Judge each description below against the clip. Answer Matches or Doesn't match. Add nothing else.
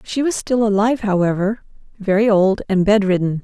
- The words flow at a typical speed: Matches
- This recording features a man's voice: Doesn't match